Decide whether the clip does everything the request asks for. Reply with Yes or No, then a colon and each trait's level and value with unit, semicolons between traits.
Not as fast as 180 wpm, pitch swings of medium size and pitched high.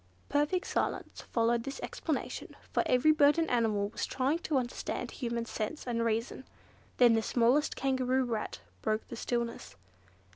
Yes: average, 150 wpm; average, 3.0 semitones; high, 245 Hz